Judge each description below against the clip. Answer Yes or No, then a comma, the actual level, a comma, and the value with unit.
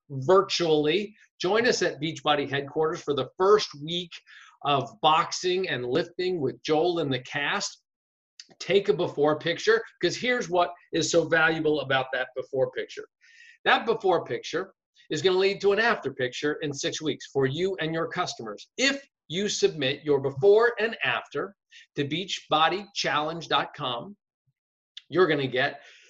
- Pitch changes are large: Yes, wide, 6.0 semitones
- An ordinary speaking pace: Yes, average, 150 wpm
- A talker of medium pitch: Yes, medium, 175 Hz